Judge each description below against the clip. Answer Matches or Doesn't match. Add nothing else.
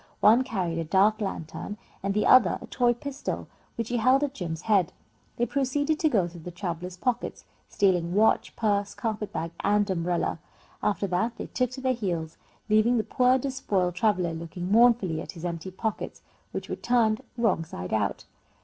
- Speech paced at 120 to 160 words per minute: Doesn't match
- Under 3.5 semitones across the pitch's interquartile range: Doesn't match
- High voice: Matches